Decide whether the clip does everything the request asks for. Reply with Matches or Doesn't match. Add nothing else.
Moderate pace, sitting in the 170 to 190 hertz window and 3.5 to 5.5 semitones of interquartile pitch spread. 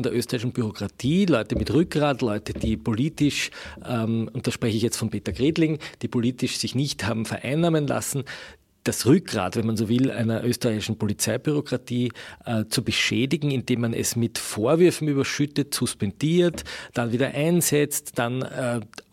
Doesn't match